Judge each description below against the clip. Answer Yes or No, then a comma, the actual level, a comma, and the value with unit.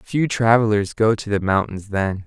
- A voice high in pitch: No, low, 105 Hz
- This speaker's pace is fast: No, average, 185 wpm